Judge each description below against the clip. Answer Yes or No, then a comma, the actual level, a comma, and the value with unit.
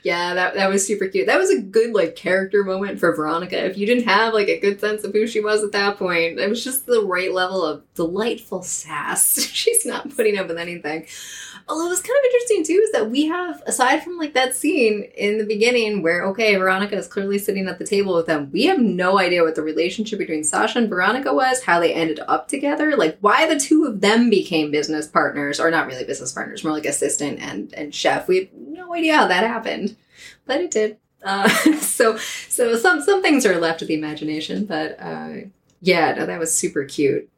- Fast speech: Yes, fast, 225 wpm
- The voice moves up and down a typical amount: No, wide, 8.4 semitones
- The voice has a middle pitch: No, high, 205 Hz